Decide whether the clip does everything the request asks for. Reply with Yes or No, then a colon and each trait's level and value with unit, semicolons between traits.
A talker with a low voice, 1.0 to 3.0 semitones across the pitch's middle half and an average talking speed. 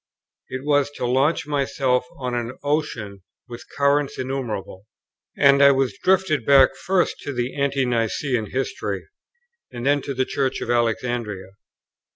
Yes: low, 130 Hz; average, 2.7 semitones; average, 145 wpm